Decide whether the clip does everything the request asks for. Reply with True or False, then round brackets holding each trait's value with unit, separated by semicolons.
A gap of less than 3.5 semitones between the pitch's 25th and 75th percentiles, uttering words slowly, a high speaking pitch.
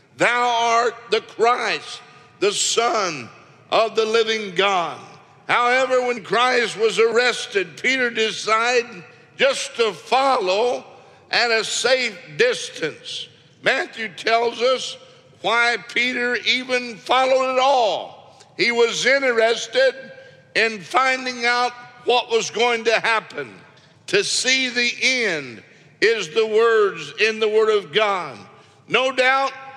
True (2.6 semitones; 115 wpm; 245 Hz)